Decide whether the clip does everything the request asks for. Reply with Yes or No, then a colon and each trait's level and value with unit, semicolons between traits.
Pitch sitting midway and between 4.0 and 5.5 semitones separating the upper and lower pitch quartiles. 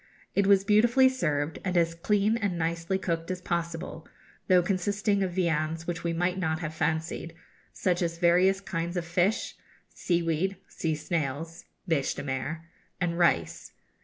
No: medium, 170 Hz; narrow, 2.6 semitones